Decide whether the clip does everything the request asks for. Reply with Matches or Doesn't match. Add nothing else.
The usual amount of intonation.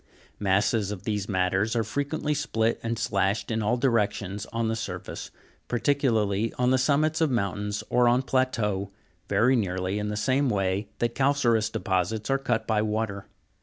Matches